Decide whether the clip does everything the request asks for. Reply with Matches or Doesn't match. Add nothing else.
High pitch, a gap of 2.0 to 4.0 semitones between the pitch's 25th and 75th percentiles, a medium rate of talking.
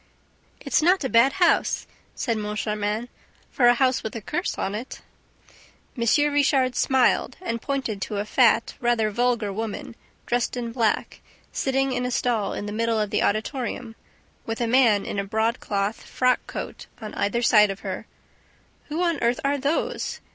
Matches